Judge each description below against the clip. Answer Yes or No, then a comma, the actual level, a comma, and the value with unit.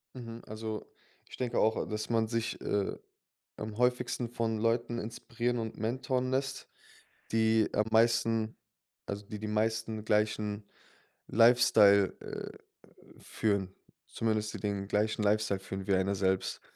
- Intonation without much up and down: Yes, narrow, 1.8 semitones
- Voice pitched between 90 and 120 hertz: Yes, low, 110 Hz